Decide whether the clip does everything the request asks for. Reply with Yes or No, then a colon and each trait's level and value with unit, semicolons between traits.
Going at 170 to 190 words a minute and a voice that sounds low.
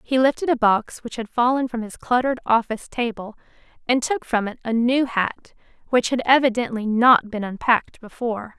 No: average, 180 wpm; high, 235 Hz